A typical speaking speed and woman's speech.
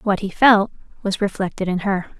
Yes: average, 190 wpm; female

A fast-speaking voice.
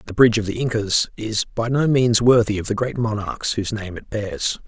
Yes: fast, 230 wpm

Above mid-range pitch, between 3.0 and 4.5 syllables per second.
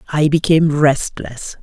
No: medium, 150 Hz; 4.4 syllables/s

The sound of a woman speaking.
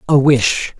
No: male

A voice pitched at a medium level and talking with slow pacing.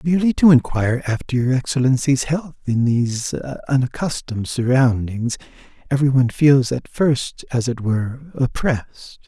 No: low, 130 Hz; slow, 130 wpm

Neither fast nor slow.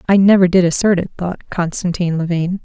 Yes: average, 180 wpm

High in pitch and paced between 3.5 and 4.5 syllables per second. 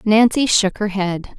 Yes: high, 205 Hz; 3.9 syllables/s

